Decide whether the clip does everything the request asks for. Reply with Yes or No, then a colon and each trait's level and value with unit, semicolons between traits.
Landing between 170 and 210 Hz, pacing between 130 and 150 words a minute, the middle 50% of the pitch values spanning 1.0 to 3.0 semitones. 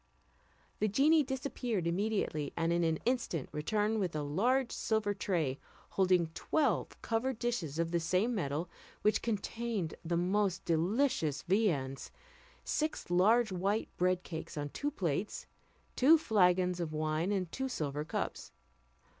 No: medium, 185 Hz; average, 140 wpm; wide, 5.5 semitones